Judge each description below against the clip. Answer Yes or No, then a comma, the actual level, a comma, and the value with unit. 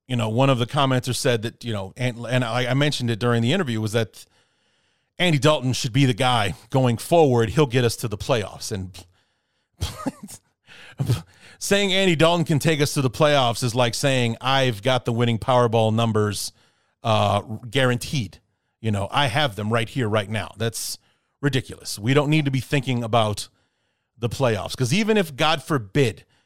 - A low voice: Yes, low, 125 Hz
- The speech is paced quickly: No, average, 185 wpm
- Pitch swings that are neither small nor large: Yes, average, 3.7 semitones